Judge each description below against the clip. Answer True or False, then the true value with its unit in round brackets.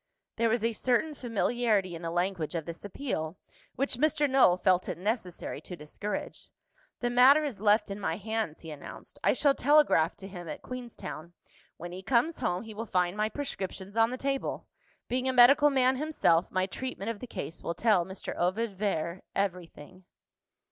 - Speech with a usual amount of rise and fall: False (5.8 semitones)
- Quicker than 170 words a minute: True (180 wpm)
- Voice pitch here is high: True (210 Hz)